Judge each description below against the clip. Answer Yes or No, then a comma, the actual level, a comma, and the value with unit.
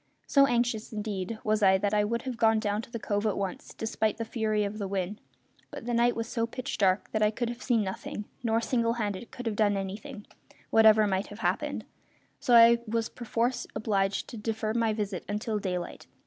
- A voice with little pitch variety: Yes, narrow, 2.1 semitones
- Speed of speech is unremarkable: No, fast, 215 wpm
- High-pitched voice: Yes, high, 220 Hz